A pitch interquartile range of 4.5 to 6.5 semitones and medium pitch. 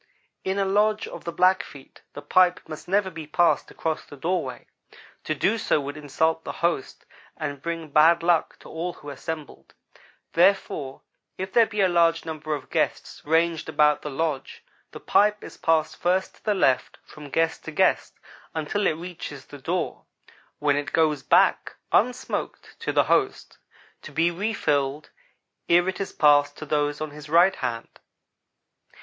No: average, 3.5 semitones; medium, 160 Hz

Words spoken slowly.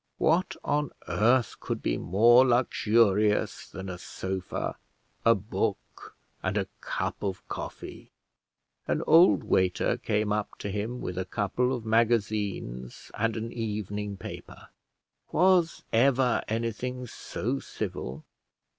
Yes: slow, 120 wpm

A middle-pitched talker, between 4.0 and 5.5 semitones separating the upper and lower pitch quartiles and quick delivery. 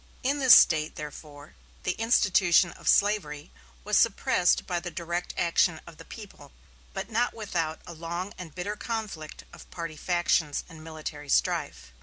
No: medium, 175 Hz; average, 4.5 semitones; average, 155 wpm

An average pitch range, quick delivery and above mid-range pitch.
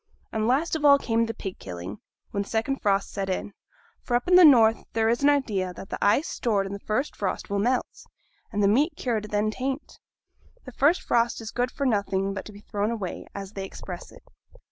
Yes: average, 4.2 semitones; fast, 225 wpm; high, 220 Hz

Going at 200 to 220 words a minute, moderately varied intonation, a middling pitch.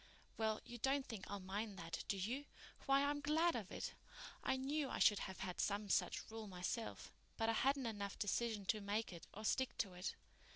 No: fast, 205 wpm; average, 4.7 semitones; high, 220 Hz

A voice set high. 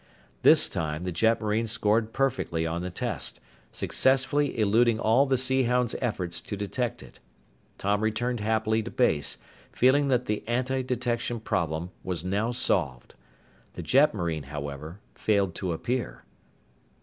No: low, 110 Hz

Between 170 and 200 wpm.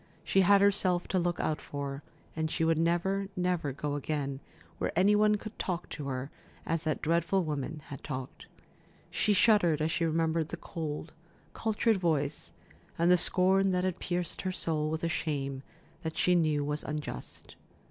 Yes: average, 175 wpm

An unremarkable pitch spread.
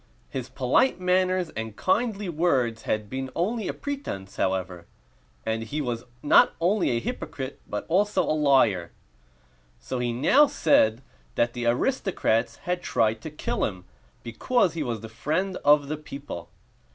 No: wide, 8.1 semitones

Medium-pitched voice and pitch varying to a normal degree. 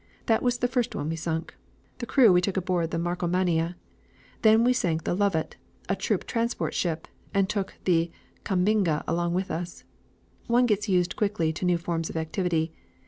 Yes: medium, 180 Hz; average, 4.0 semitones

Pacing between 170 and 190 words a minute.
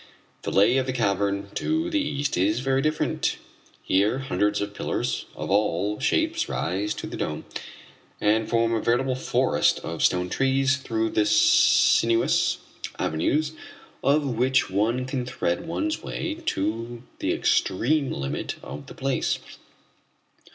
No: average, 140 wpm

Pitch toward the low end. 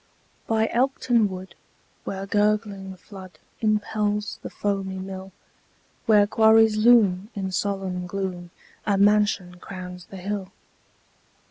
No: high, 200 Hz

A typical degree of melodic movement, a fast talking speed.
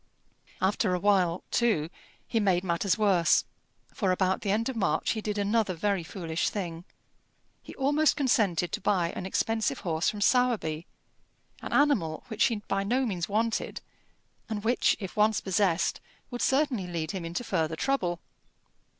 No: average, 4.3 semitones; average, 160 wpm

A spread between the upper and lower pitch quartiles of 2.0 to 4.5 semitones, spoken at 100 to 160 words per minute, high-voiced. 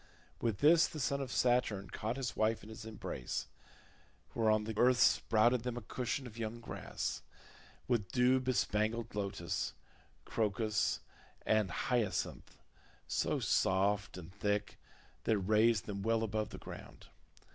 No: average, 2.7 semitones; average, 140 wpm; low, 110 Hz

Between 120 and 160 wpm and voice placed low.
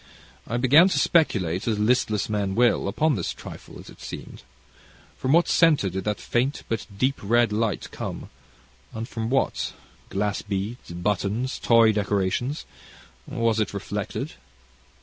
Yes: average, 145 wpm; low, 110 Hz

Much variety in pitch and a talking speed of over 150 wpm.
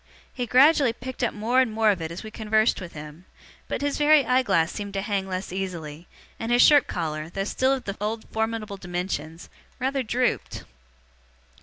Yes: wide, 5.7 semitones; average, 190 wpm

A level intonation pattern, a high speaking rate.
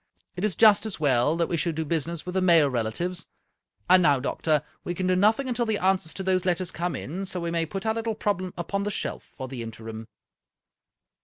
No: average, 3.8 semitones; fast, 220 wpm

